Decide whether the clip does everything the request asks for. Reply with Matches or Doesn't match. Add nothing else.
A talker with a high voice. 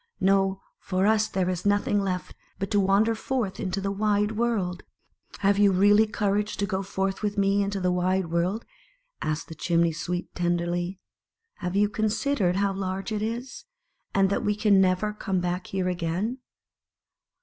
Matches